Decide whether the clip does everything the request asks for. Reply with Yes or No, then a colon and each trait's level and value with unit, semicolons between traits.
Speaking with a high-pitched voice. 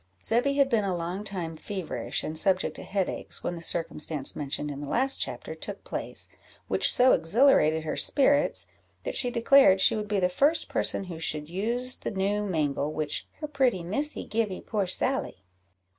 Yes: high, 195 Hz